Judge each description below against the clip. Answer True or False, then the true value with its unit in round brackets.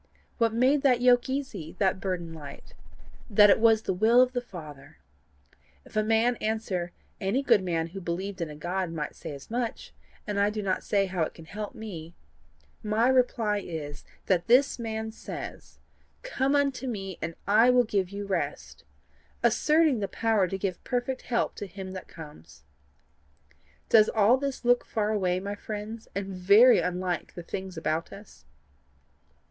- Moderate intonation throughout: True (4.4 semitones)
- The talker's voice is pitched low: False (205 Hz)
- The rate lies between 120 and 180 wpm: True (170 wpm)